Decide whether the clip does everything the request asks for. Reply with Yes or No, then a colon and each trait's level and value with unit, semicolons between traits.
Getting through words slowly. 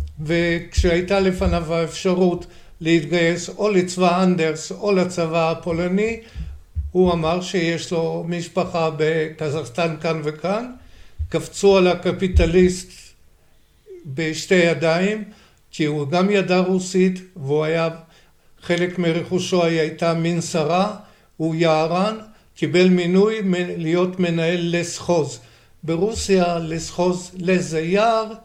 Yes: slow, 95 wpm